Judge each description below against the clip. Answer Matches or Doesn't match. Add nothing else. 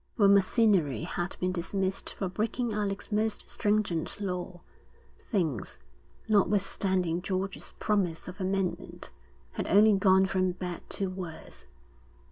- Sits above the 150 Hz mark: Matches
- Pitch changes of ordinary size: Doesn't match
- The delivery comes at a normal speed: Doesn't match